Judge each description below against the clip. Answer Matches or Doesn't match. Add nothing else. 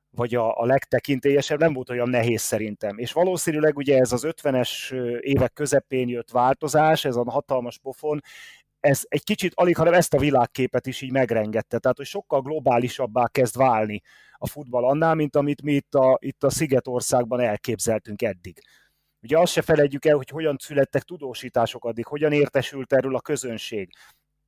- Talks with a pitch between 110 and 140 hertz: Matches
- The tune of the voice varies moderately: Matches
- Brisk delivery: Matches